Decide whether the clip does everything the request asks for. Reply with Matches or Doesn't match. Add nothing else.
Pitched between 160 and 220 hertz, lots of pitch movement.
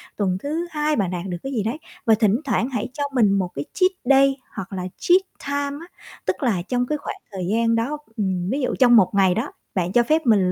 Doesn't match